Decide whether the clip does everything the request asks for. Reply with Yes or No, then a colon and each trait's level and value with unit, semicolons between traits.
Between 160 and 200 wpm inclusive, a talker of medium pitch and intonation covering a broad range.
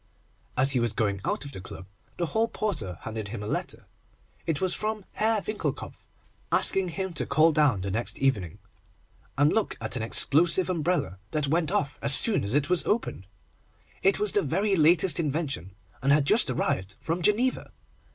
Yes: average, 180 wpm; medium, 150 Hz; wide, 8.3 semitones